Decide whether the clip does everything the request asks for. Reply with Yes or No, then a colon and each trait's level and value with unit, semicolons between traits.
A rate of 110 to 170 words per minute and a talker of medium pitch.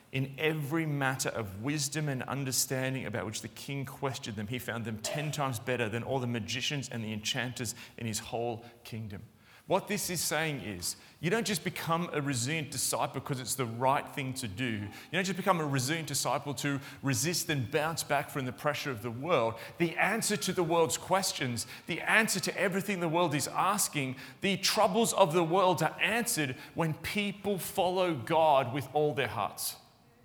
No: average, 190 wpm; medium, 145 Hz